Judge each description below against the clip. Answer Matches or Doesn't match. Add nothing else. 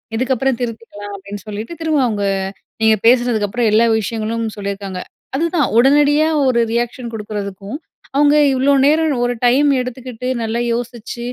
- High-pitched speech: Matches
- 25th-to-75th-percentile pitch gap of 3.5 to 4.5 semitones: Matches